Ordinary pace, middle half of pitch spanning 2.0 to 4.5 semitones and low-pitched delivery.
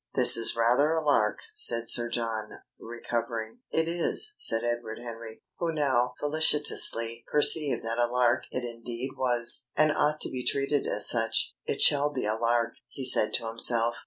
Yes: average, 170 wpm; average, 3.5 semitones; low, 120 Hz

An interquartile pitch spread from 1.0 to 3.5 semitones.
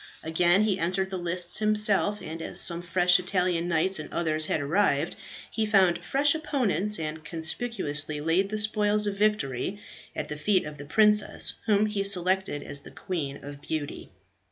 No: average, 4.6 semitones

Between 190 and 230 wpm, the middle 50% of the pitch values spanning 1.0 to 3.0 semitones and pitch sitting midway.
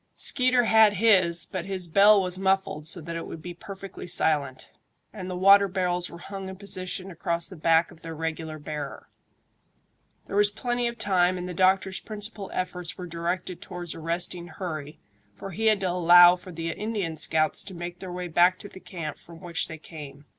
Yes: average, 195 wpm; average, 2.7 semitones; medium, 180 Hz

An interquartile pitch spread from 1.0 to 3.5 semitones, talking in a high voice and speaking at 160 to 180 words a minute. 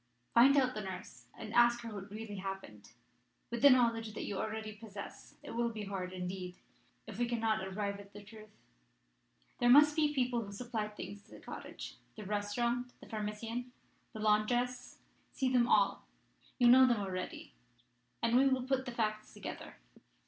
Yes: average, 3.1 semitones; high, 220 Hz; average, 175 wpm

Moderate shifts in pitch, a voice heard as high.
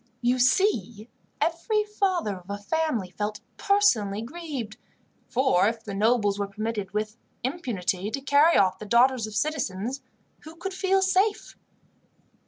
No: wide, 8.0 semitones; high, 240 Hz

